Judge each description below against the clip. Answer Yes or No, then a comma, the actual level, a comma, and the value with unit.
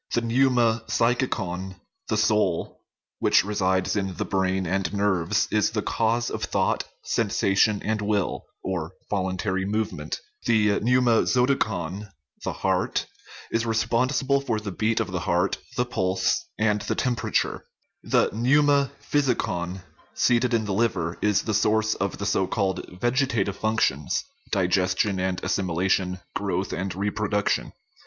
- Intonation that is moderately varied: Yes, average, 3.6 semitones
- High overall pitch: No, low, 105 Hz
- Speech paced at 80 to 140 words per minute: Yes, slow, 135 wpm